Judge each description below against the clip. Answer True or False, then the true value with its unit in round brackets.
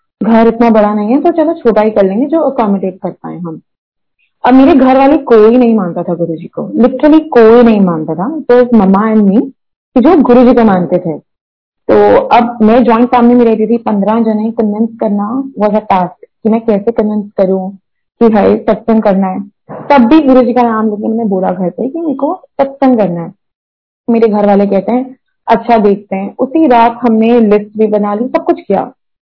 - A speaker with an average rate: False (205 wpm)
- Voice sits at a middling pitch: False (225 Hz)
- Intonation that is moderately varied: True (3.5 semitones)